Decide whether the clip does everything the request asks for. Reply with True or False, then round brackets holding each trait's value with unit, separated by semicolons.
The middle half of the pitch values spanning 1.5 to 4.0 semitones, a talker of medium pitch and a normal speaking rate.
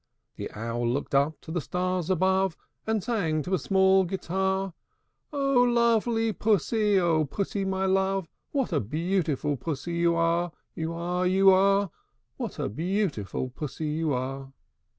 True (3.7 semitones; 180 Hz; 150 wpm)